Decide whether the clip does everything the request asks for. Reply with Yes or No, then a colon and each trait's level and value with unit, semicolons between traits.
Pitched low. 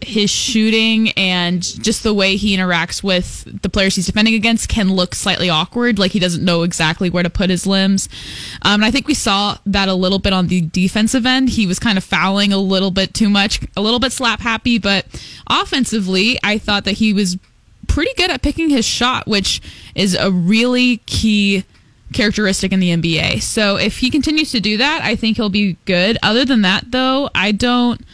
No: high, 205 Hz